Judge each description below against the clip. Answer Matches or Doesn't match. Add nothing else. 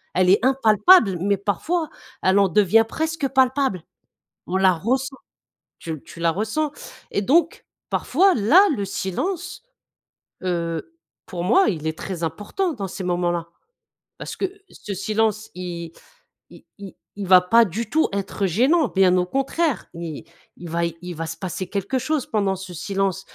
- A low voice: Doesn't match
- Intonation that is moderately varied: Doesn't match